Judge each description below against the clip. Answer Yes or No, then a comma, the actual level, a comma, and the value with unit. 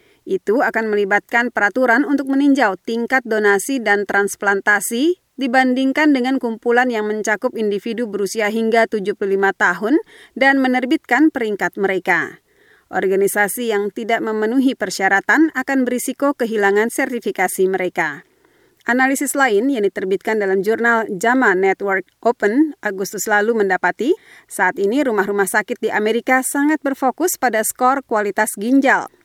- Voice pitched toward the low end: No, high, 230 Hz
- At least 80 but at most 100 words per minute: No, average, 120 wpm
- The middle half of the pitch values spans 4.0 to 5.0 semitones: Yes, average, 4.6 semitones